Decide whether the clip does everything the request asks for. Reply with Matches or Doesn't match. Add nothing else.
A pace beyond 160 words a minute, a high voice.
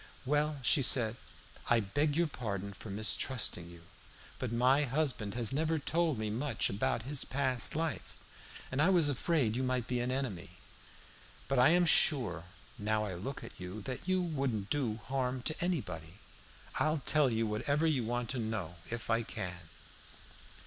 Doesn't match